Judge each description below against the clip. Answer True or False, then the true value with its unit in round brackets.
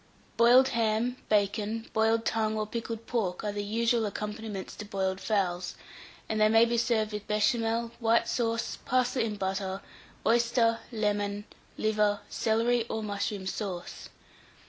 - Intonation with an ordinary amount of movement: False (2.0 semitones)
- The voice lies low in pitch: False (220 Hz)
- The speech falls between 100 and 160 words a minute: True (140 wpm)